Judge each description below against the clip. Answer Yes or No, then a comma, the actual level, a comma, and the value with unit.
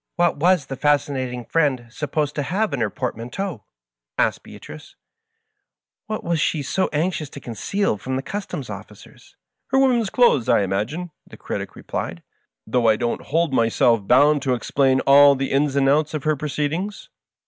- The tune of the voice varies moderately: Yes, average, 4.7 semitones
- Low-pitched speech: No, medium, 145 Hz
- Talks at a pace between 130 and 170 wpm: No, average, 190 wpm